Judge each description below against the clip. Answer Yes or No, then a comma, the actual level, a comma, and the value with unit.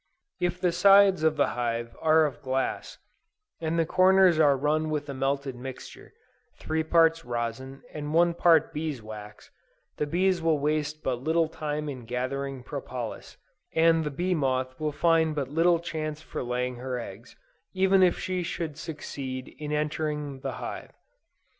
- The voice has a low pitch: No, medium, 150 Hz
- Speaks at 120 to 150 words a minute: No, average, 160 wpm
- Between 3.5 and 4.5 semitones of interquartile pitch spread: Yes, average, 3.8 semitones